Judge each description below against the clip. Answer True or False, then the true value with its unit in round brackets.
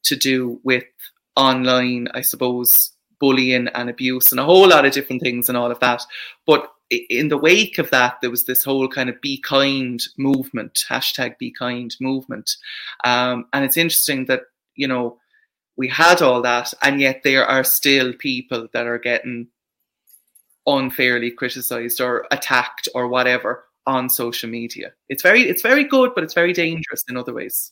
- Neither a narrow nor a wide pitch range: False (2.1 semitones)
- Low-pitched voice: True (130 Hz)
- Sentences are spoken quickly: False (175 wpm)